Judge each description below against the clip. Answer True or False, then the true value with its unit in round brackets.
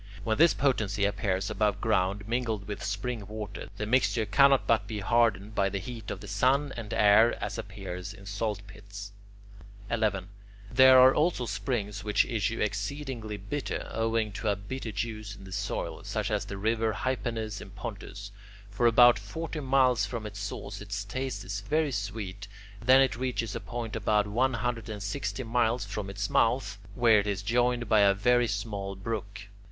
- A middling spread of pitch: True (3.1 semitones)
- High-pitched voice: False (110 Hz)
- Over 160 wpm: True (180 wpm)